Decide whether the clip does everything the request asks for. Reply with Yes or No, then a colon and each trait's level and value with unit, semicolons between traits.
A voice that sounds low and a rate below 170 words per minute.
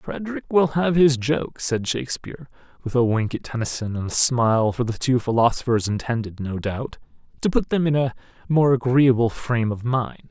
No: low, 125 Hz; average, 185 wpm